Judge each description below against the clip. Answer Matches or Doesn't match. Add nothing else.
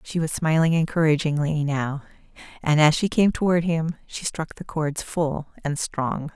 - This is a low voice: Doesn't match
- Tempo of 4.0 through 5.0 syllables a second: Matches